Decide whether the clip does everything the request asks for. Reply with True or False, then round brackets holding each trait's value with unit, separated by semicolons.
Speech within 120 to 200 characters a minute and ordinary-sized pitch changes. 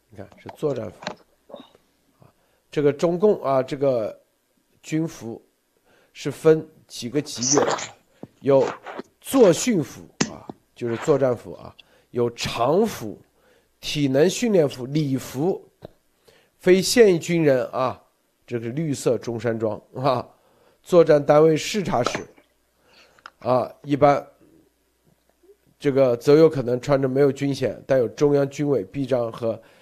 True (175 characters per minute; 4.2 semitones)